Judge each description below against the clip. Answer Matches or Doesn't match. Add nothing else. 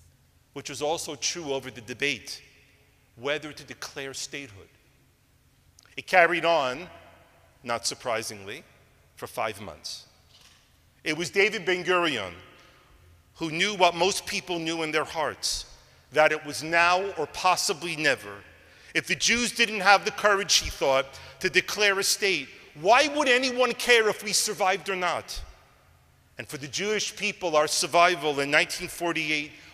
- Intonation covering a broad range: Matches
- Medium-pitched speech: Matches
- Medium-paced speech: Matches